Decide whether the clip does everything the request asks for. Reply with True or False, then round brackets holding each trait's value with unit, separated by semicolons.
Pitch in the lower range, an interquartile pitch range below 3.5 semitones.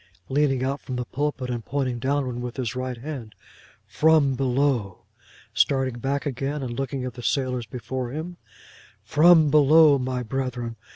True (130 Hz; 2.5 semitones)